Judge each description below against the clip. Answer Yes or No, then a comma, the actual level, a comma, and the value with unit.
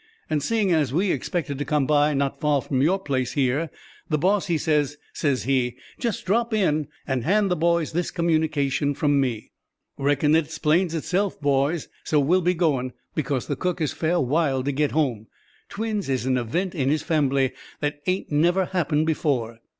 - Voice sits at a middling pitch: Yes, medium, 150 Hz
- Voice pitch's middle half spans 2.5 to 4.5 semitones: Yes, average, 3.8 semitones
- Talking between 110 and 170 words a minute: No, average, 185 wpm